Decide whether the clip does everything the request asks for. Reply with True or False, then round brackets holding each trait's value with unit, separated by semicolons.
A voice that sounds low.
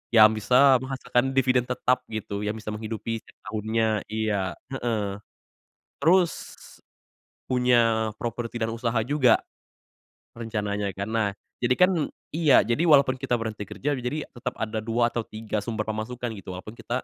True (115 Hz)